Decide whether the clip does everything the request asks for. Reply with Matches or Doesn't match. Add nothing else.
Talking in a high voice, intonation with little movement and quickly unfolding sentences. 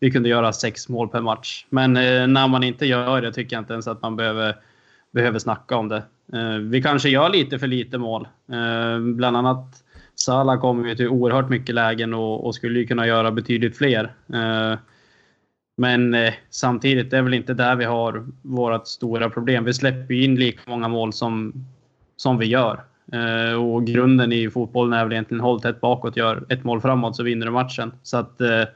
Doesn't match